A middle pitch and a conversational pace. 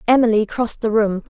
No: high, 220 Hz; average, 180 wpm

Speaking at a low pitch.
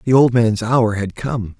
Yes: low, 115 Hz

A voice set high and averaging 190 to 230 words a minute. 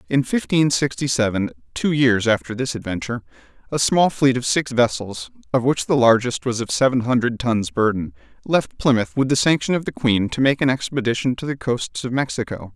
No: low, 125 Hz; average, 200 wpm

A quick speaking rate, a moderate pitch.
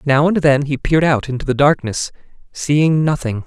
No: average, 190 wpm; medium, 145 Hz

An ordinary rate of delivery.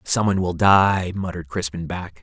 Yes: average, 160 wpm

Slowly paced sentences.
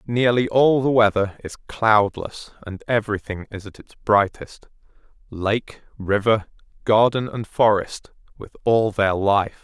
Yes: slow, 125 wpm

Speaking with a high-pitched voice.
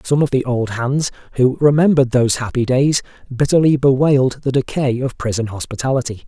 No: low, 130 Hz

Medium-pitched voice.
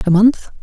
No: high, 210 Hz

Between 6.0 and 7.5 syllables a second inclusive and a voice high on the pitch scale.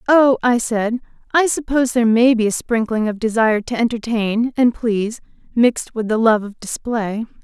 No: 5.2 syllables/s; high, 230 Hz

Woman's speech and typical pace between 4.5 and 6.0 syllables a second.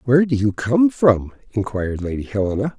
No: male; 5.6 syllables/s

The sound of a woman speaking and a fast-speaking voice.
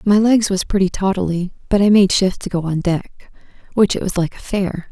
Yes: female; fast, 230 wpm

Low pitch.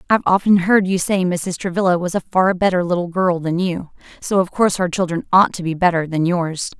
No: medium, 180 Hz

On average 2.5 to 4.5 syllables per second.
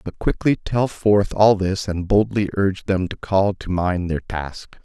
Yes: 4.2 syllables/s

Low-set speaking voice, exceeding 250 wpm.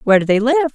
No: very high, 250 Hz; fast, 325 wpm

